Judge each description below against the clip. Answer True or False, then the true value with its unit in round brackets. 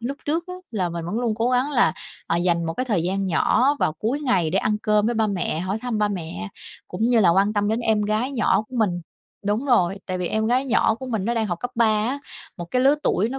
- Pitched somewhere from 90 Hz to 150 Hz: False (215 Hz)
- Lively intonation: False (4.9 semitones)